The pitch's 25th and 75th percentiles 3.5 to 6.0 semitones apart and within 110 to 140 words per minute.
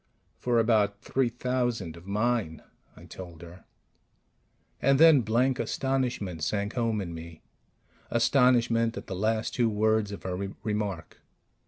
Yes: average, 4.1 semitones; slow, 135 wpm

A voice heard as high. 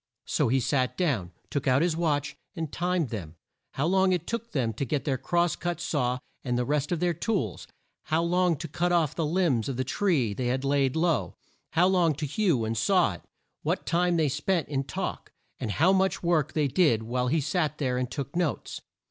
No: medium, 150 Hz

